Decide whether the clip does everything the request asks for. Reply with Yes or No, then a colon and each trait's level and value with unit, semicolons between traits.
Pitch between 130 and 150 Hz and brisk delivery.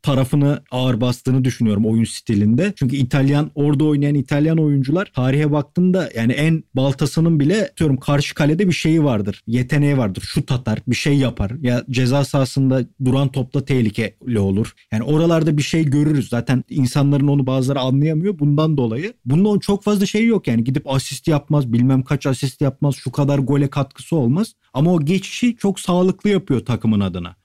Yes: medium, 140 Hz; fast, 165 wpm